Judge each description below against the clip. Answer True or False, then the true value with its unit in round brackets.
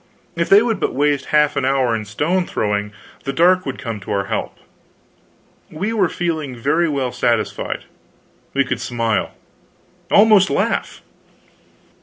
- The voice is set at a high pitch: False (145 Hz)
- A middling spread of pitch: False (6.8 semitones)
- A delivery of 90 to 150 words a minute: True (145 wpm)